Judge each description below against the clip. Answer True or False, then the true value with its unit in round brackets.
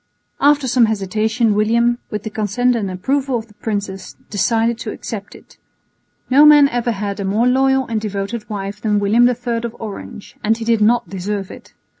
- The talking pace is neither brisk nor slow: True (185 wpm)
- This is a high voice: True (225 Hz)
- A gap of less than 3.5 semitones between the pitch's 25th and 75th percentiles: True (2.8 semitones)